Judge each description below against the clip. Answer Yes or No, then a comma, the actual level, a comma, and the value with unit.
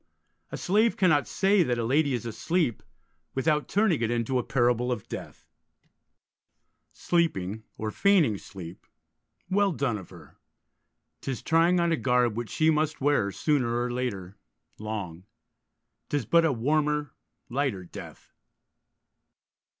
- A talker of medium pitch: No, low, 130 Hz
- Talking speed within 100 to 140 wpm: Yes, slow, 135 wpm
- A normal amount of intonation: No, wide, 5.9 semitones